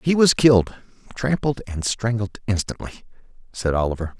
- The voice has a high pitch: No, low, 110 Hz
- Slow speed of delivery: Yes, slow, 115 wpm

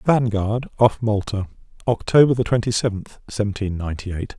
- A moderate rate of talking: No, slow, 125 wpm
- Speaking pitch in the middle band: No, low, 110 Hz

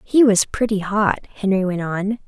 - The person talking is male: No, female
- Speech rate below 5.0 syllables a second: Yes, 4.6 syllables/s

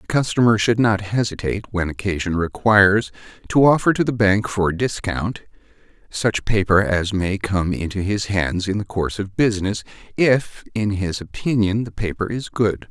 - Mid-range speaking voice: No, low, 100 Hz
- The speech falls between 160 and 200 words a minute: Yes, average, 165 wpm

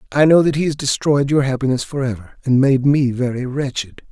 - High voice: No, low, 135 Hz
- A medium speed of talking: No, fast, 220 wpm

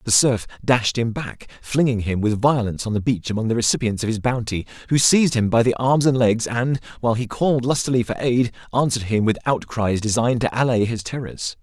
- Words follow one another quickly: Yes, fast, 215 wpm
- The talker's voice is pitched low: Yes, low, 120 Hz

